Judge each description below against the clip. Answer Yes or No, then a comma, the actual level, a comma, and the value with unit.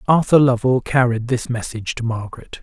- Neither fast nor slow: Yes, average, 160 wpm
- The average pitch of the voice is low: Yes, low, 120 Hz